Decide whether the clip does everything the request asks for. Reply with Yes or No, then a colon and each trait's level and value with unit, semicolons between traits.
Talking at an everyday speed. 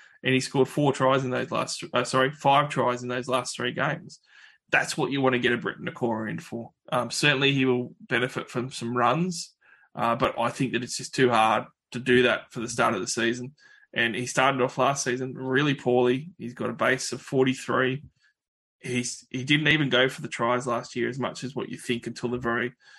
No: fast, 225 wpm